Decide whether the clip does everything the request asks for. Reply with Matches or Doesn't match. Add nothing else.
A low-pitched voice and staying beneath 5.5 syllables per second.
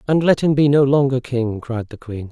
Matches